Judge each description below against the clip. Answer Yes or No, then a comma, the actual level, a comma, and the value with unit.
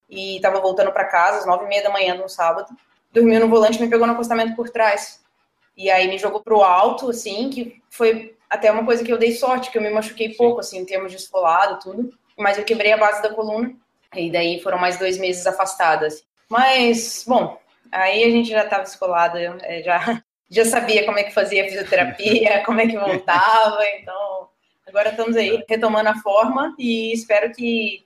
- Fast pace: Yes, fast, 205 wpm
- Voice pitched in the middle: No, high, 210 Hz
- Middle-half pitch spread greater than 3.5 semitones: No, average, 3.2 semitones